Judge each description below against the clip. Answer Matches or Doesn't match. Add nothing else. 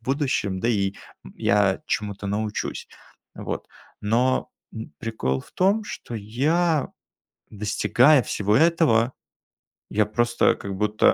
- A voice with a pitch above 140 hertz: Doesn't match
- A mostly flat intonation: Doesn't match